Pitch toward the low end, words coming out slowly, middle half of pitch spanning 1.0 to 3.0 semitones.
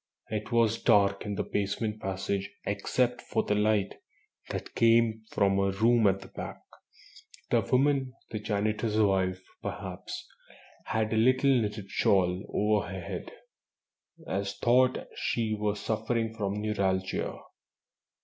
Yes: low, 105 Hz; slow, 130 wpm; narrow, 2.5 semitones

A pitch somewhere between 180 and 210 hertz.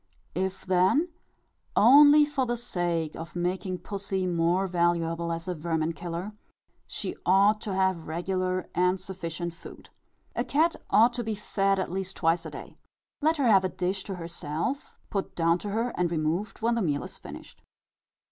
Yes: medium, 185 Hz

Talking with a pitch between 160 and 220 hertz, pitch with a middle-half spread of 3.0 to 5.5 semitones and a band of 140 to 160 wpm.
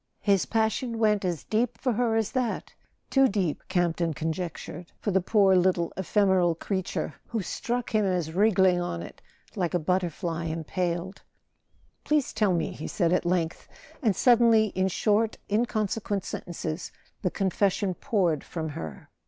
Yes: high, 190 Hz; average, 3.9 semitones; average, 150 wpm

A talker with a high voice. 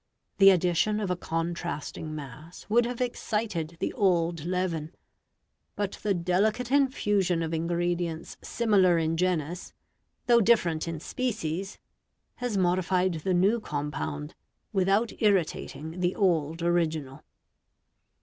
No: medium, 180 Hz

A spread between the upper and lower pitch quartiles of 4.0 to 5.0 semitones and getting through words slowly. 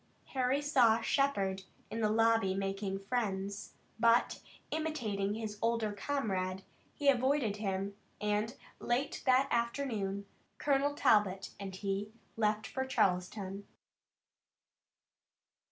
Yes: average, 4.3 semitones; slow, 105 wpm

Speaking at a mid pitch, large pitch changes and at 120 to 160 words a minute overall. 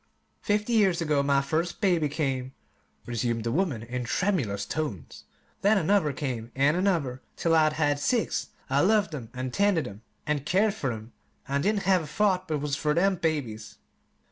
No: medium, 150 Hz; wide, 6.3 semitones; average, 175 wpm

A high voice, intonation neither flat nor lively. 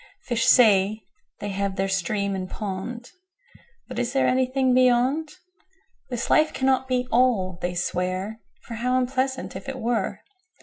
Yes: high, 245 Hz; average, 4.8 semitones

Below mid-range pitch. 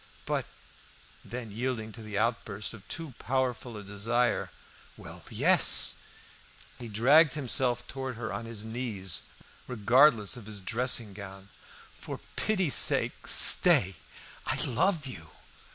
Yes: low, 115 Hz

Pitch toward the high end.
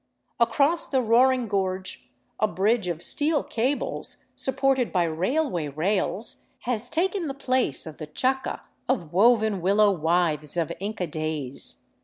Yes: high, 210 Hz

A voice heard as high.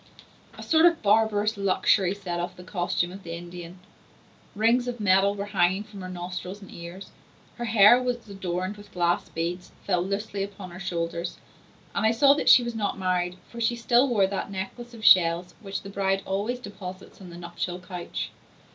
Yes: high, 195 Hz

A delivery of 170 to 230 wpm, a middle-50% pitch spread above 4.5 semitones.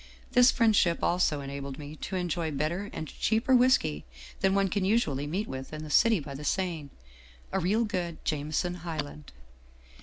Yes: average, 175 wpm; average, 5.0 semitones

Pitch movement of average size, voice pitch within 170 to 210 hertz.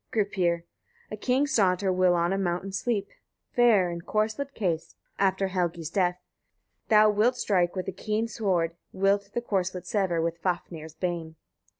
Yes: average, 3.4 semitones; high, 190 Hz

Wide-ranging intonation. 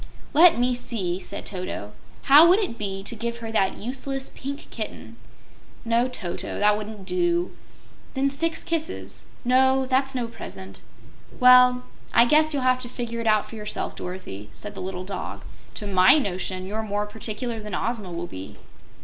No: average, 4.9 semitones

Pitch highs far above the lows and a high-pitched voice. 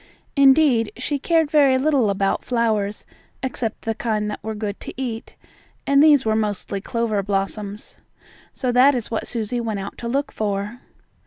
No: average, 4.0 semitones; high, 230 Hz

